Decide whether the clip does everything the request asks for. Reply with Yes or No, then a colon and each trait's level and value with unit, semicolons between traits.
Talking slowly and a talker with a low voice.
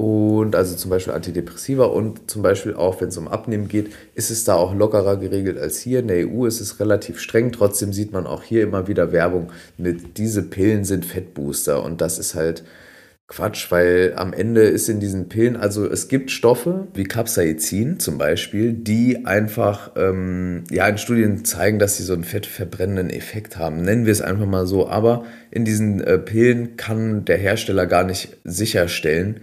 No: fast, 190 wpm; low, 100 Hz